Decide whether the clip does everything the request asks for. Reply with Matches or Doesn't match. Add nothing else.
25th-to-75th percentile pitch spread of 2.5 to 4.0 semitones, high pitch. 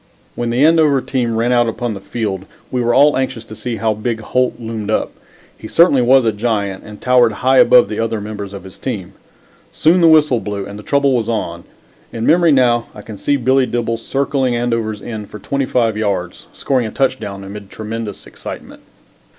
Doesn't match